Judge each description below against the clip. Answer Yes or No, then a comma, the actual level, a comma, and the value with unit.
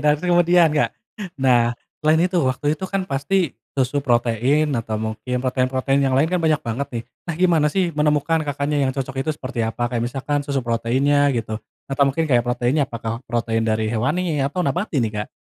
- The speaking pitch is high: No, low, 135 Hz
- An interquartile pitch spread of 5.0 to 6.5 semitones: No, average, 4.2 semitones